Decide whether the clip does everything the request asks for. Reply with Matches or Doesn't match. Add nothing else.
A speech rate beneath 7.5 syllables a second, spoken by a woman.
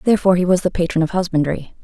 Doesn't match